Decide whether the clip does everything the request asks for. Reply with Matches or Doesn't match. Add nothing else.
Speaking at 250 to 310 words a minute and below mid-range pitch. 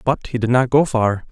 Matches